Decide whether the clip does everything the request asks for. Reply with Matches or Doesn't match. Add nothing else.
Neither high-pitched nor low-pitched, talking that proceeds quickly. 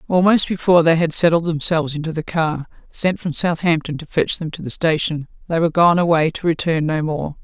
Matches